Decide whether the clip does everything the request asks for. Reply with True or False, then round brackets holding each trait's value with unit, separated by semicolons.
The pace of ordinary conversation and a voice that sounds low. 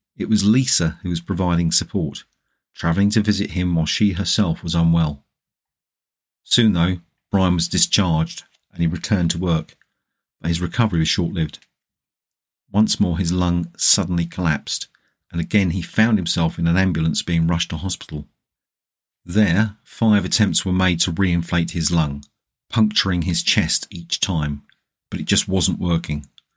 True (155 wpm; 85 Hz)